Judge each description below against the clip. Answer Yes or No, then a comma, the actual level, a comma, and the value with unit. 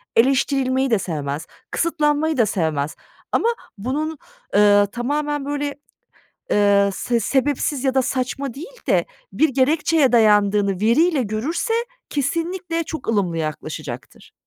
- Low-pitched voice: No, very high, 260 Hz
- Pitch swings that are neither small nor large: No, wide, 6.4 semitones